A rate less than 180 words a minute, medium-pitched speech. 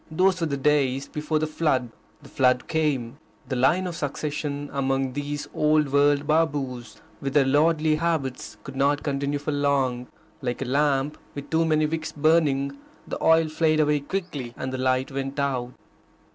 Yes: average, 170 wpm; medium, 145 Hz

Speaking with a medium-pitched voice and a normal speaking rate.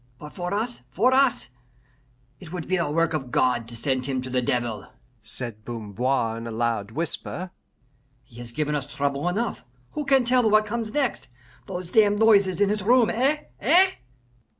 Yes: medium, 170 Hz; average, 180 wpm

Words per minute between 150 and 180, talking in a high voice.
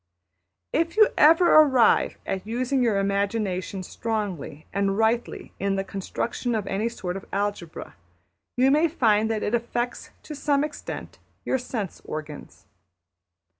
No: slow, 135 wpm; high, 220 Hz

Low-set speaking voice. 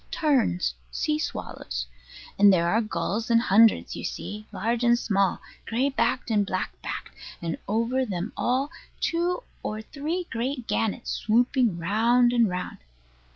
No: high, 230 Hz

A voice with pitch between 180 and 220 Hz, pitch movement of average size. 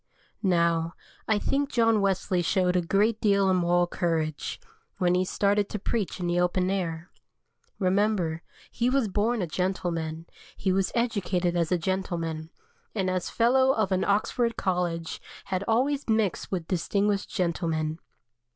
Yes: medium, 185 Hz; average, 3.2 semitones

